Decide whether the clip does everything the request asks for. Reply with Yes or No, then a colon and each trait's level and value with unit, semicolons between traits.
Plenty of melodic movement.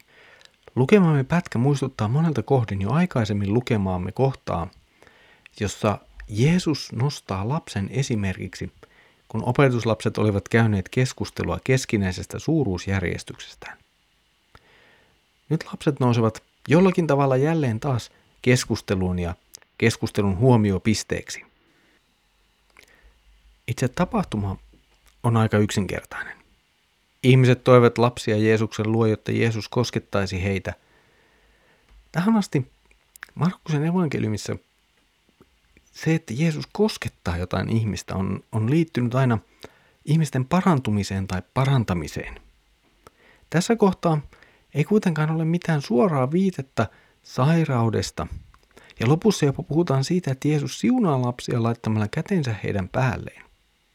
Yes: wide, 6.8 semitones